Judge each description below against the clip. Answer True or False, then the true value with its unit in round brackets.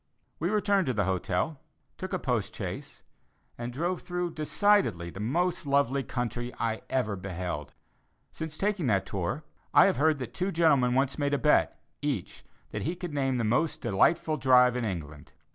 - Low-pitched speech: True (130 Hz)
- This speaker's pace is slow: False (175 wpm)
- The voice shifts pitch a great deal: True (7.1 semitones)